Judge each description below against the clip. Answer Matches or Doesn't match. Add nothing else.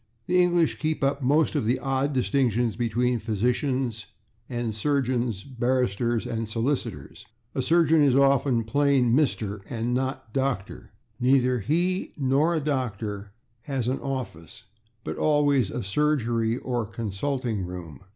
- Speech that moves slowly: Matches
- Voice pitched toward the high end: Doesn't match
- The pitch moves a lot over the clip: Doesn't match